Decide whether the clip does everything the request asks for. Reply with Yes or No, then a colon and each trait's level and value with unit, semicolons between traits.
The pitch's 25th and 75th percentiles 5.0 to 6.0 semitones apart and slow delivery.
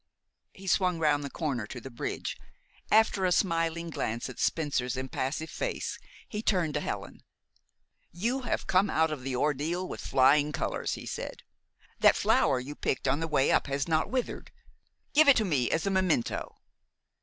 No: wide, 5.4 semitones; average, 175 wpm